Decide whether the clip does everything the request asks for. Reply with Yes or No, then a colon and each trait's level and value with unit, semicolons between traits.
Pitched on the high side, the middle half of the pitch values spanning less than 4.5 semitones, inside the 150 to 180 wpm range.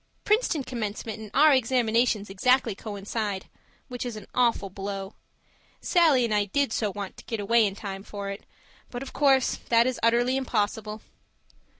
Yes: high, 225 Hz; average, 3.6 semitones; average, 165 wpm